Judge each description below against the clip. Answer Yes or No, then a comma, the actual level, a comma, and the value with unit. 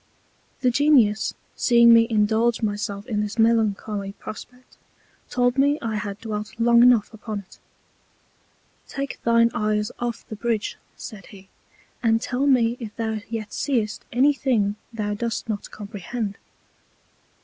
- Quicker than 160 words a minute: No, average, 140 wpm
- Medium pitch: No, high, 225 Hz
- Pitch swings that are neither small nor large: No, narrow, 2.2 semitones